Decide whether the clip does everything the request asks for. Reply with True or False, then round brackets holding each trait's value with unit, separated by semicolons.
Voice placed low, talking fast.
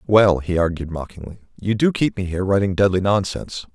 False (95 Hz; 190 wpm)